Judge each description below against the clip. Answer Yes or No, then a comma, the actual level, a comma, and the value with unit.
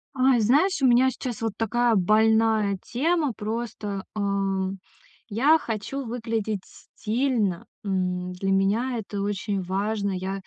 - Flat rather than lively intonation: No, average, 3.6 semitones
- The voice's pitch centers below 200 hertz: No, high, 220 Hz